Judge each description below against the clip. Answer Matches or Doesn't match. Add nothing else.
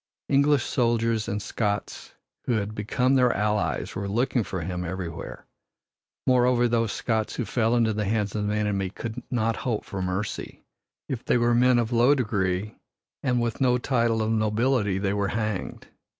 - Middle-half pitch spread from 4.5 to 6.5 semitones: Doesn't match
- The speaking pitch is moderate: Doesn't match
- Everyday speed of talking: Matches